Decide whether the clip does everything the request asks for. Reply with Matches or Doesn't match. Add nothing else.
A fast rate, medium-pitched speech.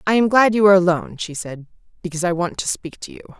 Matches